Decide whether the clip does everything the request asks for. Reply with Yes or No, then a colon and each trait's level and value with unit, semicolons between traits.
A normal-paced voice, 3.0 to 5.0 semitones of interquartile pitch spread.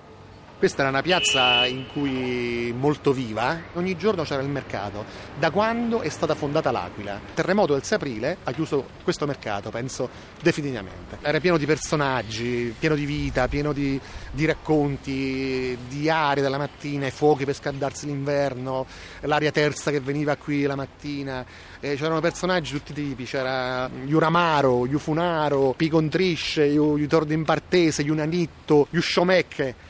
Yes: average, 145 wpm; average, 3.4 semitones